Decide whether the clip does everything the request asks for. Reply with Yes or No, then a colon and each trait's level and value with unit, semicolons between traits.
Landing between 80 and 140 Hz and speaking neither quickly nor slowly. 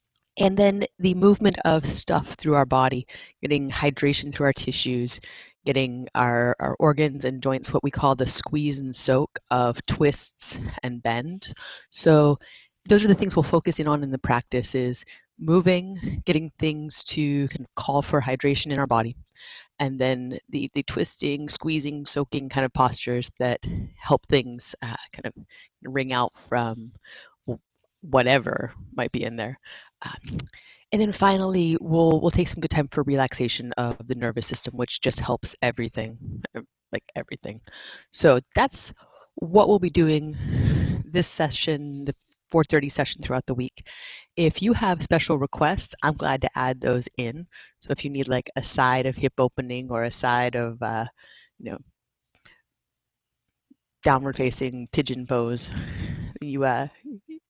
Yes: low, 135 Hz; average, 155 wpm